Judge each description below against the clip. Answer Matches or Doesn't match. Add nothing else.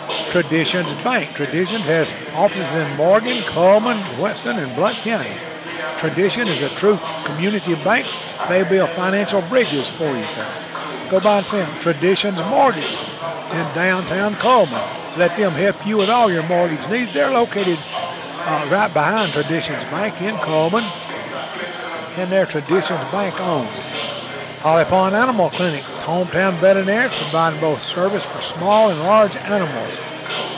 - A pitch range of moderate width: Matches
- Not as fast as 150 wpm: Matches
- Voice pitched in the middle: Matches